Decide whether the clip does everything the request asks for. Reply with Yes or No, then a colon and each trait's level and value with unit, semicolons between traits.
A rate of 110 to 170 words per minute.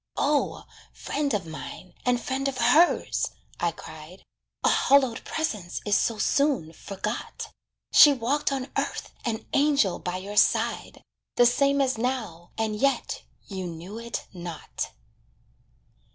Yes: slow, 135 wpm